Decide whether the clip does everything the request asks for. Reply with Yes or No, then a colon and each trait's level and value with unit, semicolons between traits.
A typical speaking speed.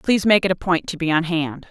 No: fast, 315 wpm